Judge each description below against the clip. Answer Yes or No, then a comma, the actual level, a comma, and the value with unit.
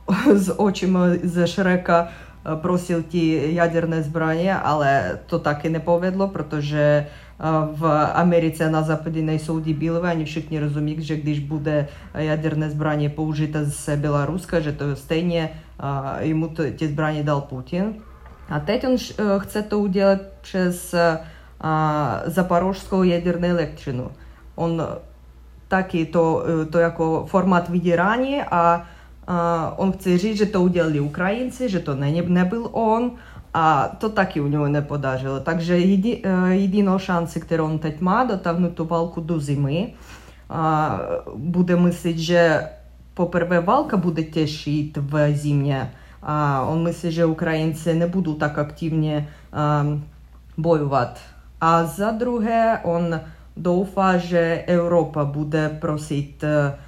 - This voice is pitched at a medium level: Yes, medium, 165 Hz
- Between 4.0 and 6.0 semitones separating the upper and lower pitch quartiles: No, average, 2.8 semitones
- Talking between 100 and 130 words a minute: Yes, average, 120 wpm